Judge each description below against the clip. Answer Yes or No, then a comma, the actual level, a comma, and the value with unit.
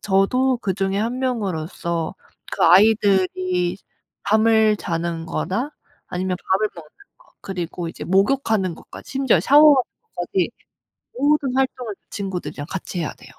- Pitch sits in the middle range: No, high, 195 Hz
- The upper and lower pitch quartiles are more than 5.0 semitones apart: Yes, wide, 5.6 semitones